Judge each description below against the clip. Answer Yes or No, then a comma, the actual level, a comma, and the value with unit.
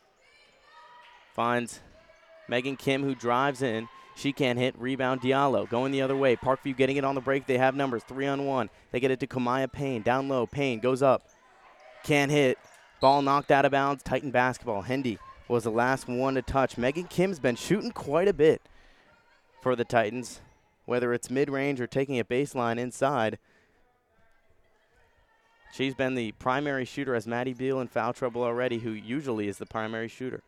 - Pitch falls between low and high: No, low, 130 Hz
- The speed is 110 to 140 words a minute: No, average, 180 wpm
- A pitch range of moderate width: No, narrow, 2.3 semitones